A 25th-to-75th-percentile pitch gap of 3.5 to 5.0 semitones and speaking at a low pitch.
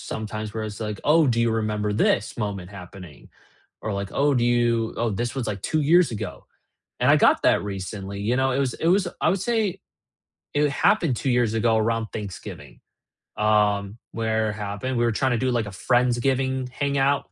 Yes: average, 4.1 semitones; low, 115 Hz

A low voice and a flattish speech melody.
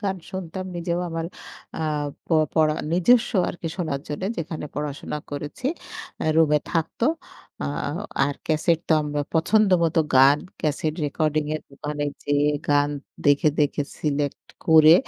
No: medium, 155 Hz; narrow, 2.3 semitones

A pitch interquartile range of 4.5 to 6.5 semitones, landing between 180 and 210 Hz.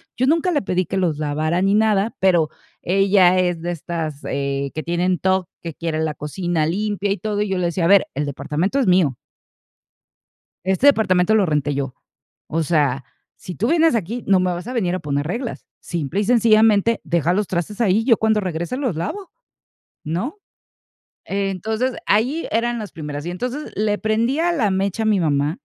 Yes: average, 4.9 semitones; medium, 185 Hz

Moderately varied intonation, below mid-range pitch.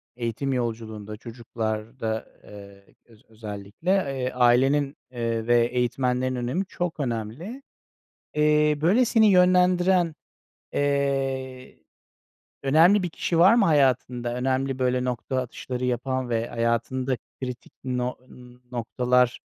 Yes: average, 3.7 semitones; low, 125 Hz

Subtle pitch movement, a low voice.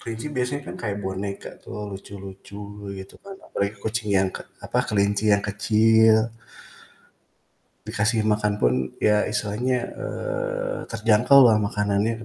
Yes: narrow, 2.3 semitones; low, 105 Hz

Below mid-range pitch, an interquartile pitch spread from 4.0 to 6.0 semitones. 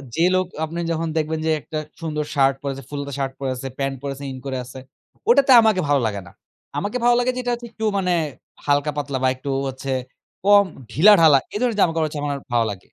No: medium, 150 Hz; average, 5.2 semitones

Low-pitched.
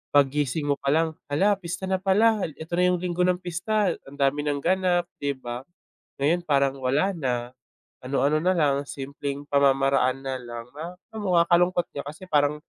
No: medium, 150 Hz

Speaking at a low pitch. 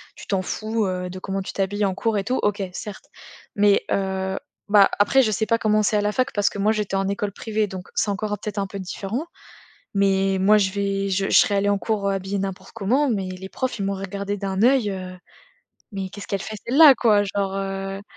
No: high, 200 Hz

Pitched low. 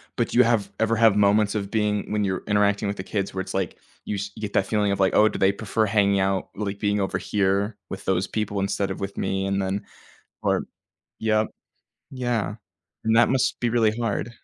Yes: low, 100 Hz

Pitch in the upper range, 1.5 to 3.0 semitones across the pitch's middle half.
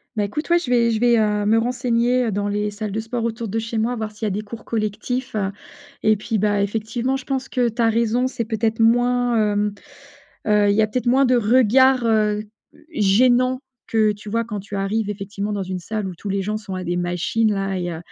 Yes: high, 220 Hz; average, 2.7 semitones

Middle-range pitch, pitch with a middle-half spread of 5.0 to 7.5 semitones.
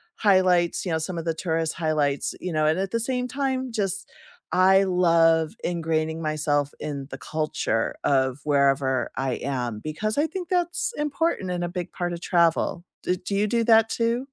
Yes: medium, 175 Hz; wide, 5.6 semitones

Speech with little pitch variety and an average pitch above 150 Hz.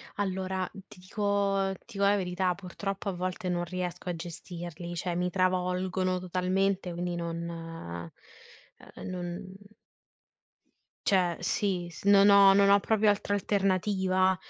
Yes: narrow, 2.0 semitones; medium, 185 Hz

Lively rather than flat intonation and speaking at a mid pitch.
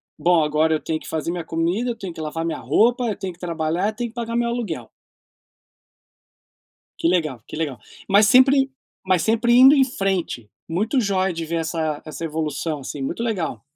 Yes: wide, 6.0 semitones; medium, 175 Hz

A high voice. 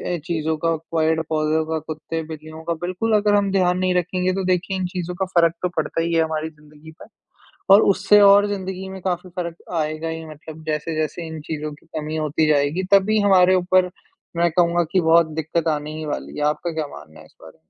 No: medium, 165 Hz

